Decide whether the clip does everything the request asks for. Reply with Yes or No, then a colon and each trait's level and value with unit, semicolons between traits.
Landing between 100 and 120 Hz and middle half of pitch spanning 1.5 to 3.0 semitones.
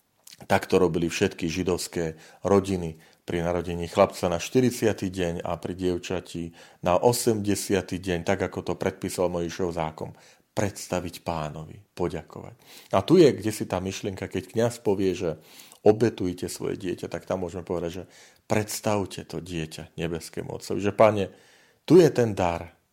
No: very low, 90 Hz; average, 2.7 semitones